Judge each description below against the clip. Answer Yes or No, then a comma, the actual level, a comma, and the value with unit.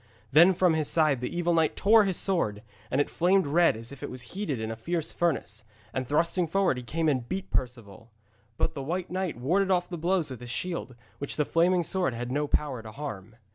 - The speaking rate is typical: No, fast, 230 wpm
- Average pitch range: No, wide, 6.0 semitones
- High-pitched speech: No, medium, 155 Hz